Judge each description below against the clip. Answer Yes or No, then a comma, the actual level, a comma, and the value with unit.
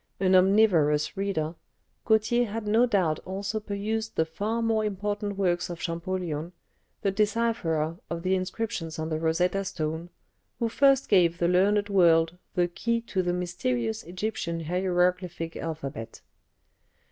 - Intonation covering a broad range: No, average, 4.0 semitones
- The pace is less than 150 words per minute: Yes, slow, 135 wpm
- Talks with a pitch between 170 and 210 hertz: Yes, medium, 185 Hz